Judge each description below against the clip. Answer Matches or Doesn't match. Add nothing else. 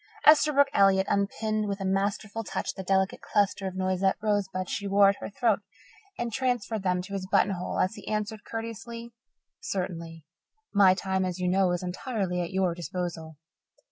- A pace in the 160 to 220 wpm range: Matches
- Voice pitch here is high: Matches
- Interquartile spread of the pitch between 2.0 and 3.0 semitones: Matches